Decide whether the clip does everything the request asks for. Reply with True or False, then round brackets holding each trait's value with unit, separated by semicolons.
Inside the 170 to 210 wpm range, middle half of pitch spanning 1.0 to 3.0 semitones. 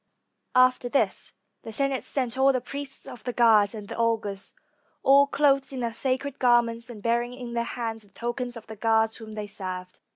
True (195 wpm; 2.6 semitones)